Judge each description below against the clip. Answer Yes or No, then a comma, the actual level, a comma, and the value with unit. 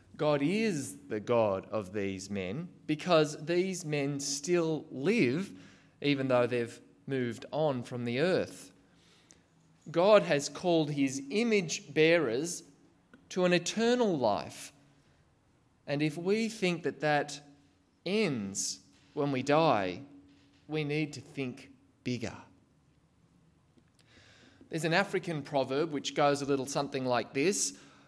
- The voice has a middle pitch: Yes, medium, 145 Hz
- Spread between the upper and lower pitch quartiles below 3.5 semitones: No, average, 4.9 semitones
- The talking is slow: Yes, slow, 120 wpm